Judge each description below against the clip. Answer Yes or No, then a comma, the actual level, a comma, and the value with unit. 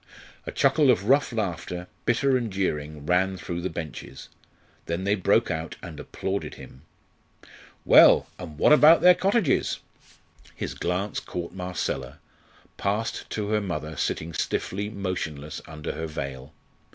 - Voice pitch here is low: Yes, very low, 95 Hz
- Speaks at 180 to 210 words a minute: No, slow, 135 wpm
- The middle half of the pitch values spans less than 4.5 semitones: No, average, 5.2 semitones